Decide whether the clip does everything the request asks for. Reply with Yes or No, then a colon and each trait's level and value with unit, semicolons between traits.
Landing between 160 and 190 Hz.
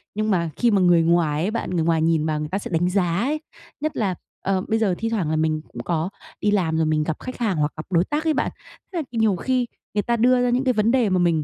Yes: medium, 185 Hz